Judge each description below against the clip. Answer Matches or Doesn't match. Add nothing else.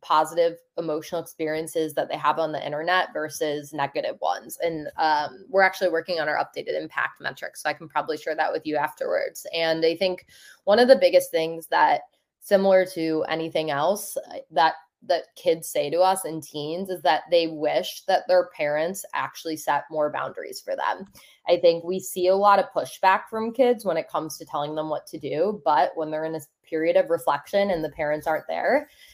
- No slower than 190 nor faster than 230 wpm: Matches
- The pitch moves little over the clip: Doesn't match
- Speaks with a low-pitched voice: Doesn't match